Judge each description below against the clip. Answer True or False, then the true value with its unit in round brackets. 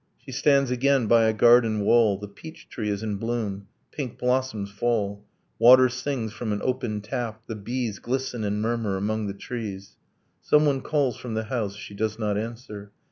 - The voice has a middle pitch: False (115 Hz)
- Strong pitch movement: False (3.3 semitones)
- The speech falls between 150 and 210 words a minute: True (180 wpm)